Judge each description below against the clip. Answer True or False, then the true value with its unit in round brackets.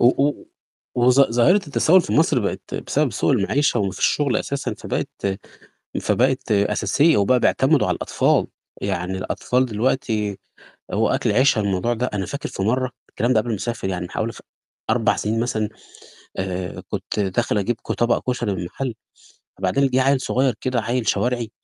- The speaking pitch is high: False (120 Hz)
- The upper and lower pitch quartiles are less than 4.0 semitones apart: False (4.3 semitones)